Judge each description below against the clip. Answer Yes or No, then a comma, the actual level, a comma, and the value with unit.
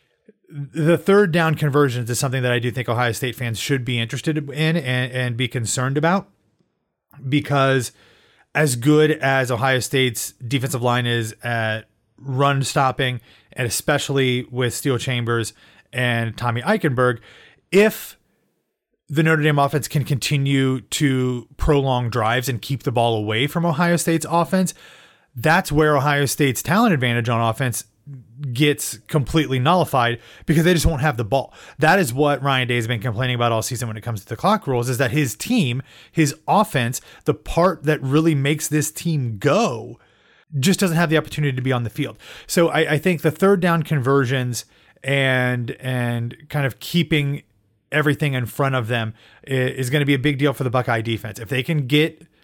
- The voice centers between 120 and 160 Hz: Yes, low, 135 Hz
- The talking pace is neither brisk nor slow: Yes, average, 175 wpm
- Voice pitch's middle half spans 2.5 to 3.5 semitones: No, average, 3.9 semitones